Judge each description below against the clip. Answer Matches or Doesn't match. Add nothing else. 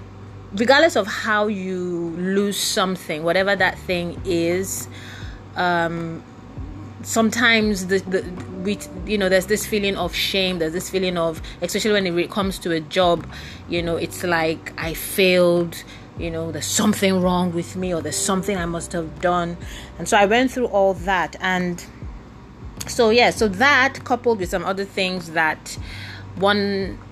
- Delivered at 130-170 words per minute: Matches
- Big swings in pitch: Doesn't match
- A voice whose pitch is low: Doesn't match